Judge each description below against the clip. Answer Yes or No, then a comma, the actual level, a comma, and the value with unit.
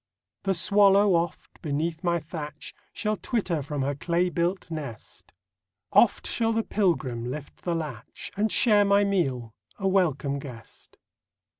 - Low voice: No, medium, 170 Hz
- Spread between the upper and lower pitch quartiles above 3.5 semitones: Yes, wide, 5.6 semitones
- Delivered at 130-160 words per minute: Yes, average, 140 wpm